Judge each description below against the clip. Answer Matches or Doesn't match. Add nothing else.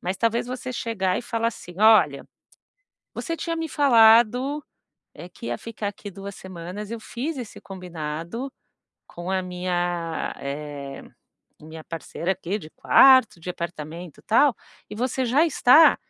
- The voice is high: Matches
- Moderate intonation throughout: Doesn't match